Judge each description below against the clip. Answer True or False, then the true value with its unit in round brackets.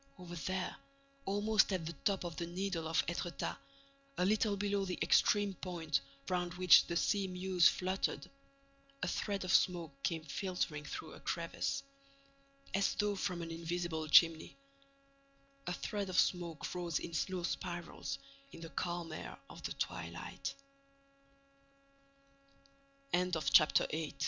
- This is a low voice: False (180 Hz)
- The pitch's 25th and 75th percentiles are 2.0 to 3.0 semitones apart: True (2.4 semitones)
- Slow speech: True (130 wpm)